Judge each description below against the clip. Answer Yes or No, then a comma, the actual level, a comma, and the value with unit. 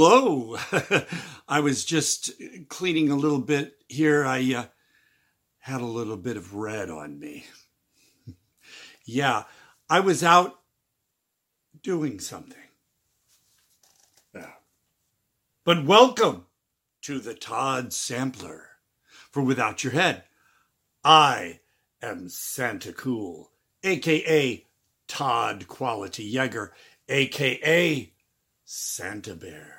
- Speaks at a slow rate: Yes, slow, 95 wpm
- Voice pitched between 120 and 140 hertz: Yes, low, 135 Hz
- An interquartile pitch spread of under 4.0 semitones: No, average, 4.7 semitones